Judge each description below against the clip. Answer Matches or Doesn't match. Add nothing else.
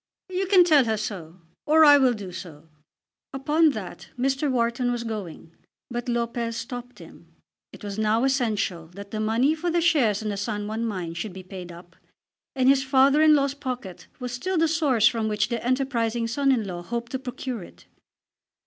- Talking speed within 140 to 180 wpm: Doesn't match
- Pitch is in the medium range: Doesn't match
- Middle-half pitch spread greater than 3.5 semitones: Matches